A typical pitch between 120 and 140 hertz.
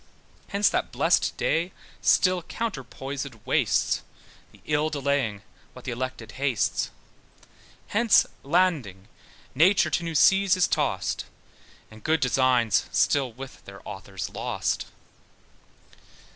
Yes: low, 135 Hz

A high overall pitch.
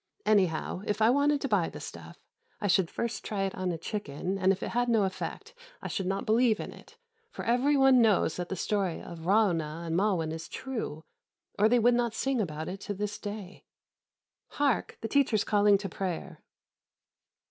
Yes: high, 205 Hz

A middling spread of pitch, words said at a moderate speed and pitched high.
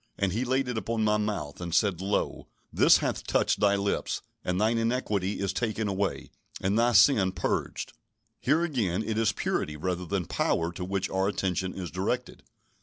No: average, 3.3 semitones; average, 180 wpm; low, 100 Hz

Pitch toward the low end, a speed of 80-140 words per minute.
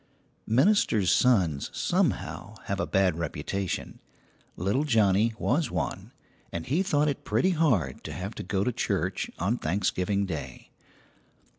Yes: low, 100 Hz; slow, 135 wpm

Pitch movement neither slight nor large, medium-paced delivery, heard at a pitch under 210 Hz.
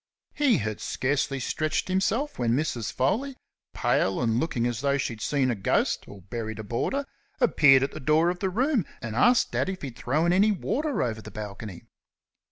No: wide, 8.6 semitones; average, 190 wpm; low, 135 Hz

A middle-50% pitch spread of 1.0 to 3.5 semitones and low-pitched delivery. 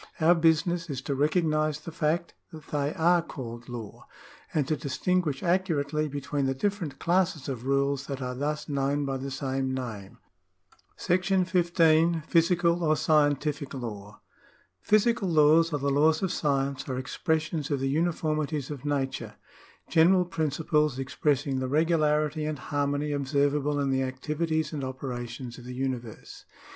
No: average, 3.2 semitones; medium, 150 Hz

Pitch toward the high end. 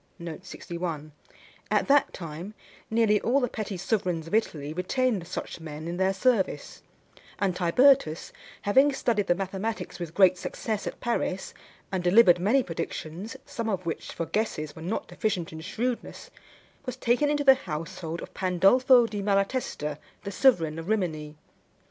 Yes: high, 195 Hz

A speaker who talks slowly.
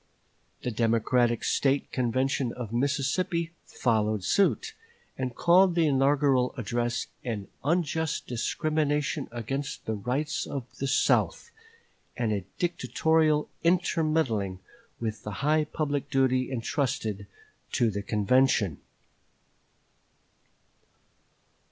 Yes: slow, 95 wpm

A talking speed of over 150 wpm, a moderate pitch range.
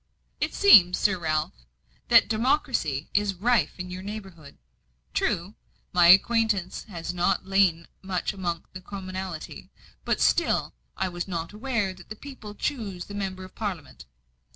No: average, 145 wpm; average, 3.0 semitones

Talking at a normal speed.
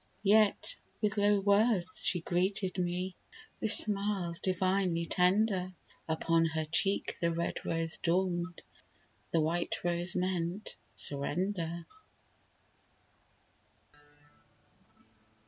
No: slow, 90 wpm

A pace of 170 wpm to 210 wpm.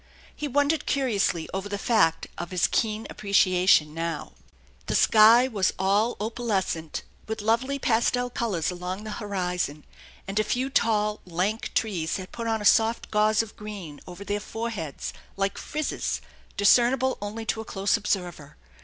No: average, 155 wpm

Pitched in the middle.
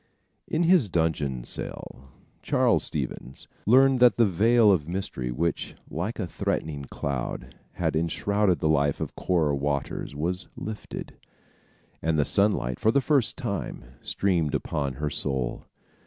No: very low, 80 Hz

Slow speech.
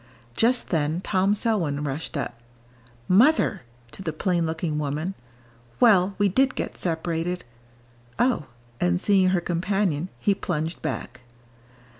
Yes: slow, 125 wpm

